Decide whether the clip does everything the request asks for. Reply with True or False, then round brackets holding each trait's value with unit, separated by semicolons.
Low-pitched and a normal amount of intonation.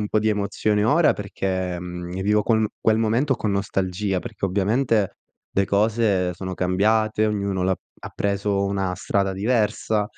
False (100 Hz; 2.3 semitones)